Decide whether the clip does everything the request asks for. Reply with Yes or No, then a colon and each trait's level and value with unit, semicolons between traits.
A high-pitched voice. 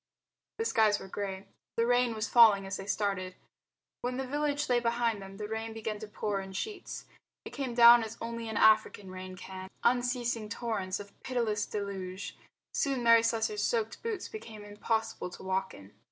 Yes: high, 220 Hz